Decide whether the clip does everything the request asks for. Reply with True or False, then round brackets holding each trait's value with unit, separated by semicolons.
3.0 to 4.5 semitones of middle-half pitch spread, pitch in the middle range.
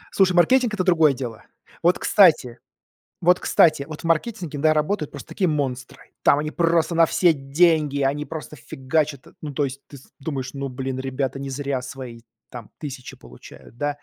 True (3.6 semitones; 145 Hz)